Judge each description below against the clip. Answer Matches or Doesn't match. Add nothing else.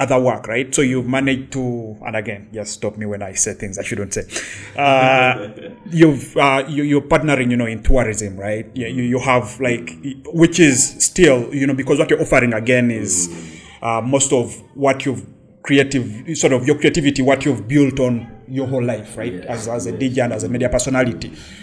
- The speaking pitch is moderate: Doesn't match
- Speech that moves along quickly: Doesn't match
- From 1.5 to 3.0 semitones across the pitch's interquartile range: Doesn't match